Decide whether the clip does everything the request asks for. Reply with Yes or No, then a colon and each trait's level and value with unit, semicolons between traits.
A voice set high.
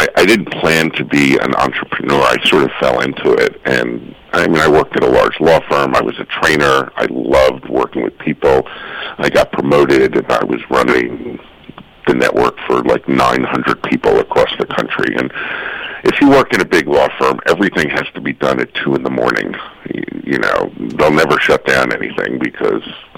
Yes: very high, 370 Hz